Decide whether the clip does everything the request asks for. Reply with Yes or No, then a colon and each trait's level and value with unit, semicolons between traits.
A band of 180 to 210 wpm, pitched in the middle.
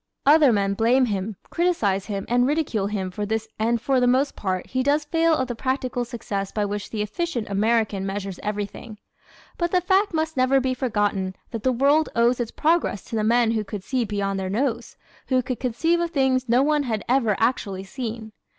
No: fast, 205 wpm; high, 235 Hz